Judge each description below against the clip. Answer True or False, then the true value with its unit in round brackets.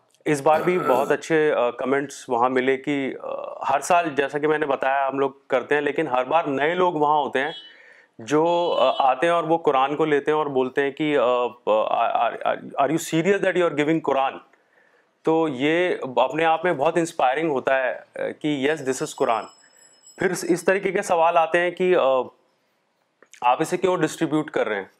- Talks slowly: False (185 wpm)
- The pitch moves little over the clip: False (3.3 semitones)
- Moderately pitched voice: True (155 Hz)